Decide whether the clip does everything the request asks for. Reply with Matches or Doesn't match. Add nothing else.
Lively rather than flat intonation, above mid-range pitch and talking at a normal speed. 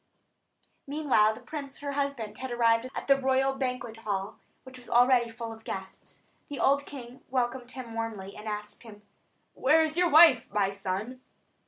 Doesn't match